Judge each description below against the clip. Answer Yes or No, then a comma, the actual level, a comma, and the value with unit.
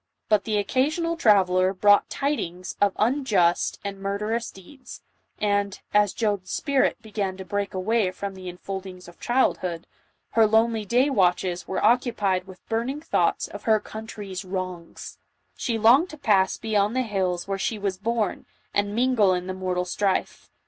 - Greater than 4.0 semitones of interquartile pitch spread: No, average, 3.3 semitones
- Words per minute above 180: No, average, 155 wpm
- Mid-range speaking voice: No, high, 205 Hz